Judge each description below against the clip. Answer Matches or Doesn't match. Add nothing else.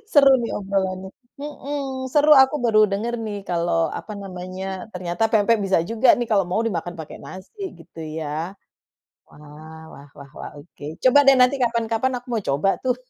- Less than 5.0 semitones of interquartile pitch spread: Doesn't match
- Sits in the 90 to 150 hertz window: Doesn't match